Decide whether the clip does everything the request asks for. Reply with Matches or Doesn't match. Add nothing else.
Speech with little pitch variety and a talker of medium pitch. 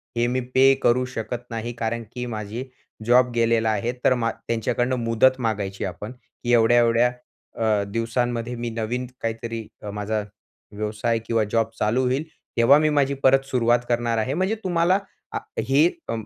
Doesn't match